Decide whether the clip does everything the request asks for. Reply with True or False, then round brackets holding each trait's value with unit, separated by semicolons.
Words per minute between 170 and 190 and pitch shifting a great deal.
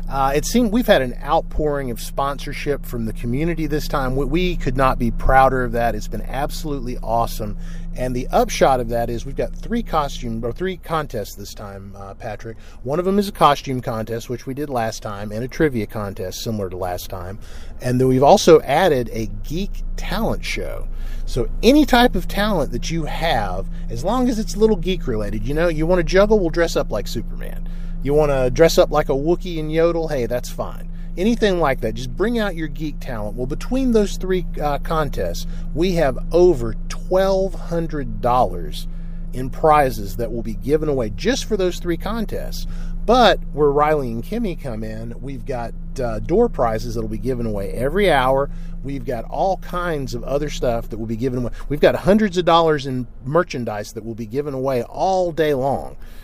False (200 wpm; 6.9 semitones)